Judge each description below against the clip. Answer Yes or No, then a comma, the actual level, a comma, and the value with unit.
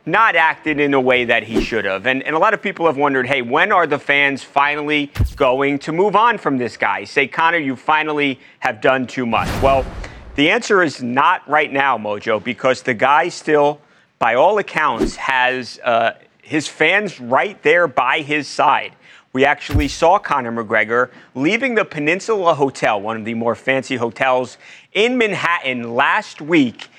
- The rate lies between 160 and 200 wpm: Yes, average, 180 wpm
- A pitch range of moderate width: Yes, average, 3.8 semitones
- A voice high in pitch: No, medium, 140 Hz